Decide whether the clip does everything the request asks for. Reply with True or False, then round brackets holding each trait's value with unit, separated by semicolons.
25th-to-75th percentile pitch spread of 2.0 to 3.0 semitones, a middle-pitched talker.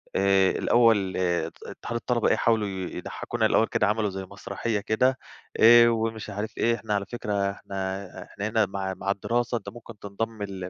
False (2.7 semitones; 105 Hz)